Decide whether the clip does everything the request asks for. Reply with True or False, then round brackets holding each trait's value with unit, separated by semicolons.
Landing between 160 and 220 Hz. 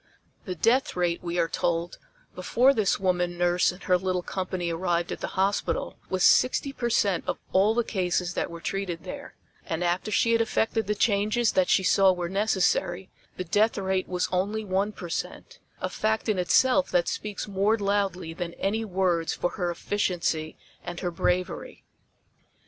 True (185 Hz)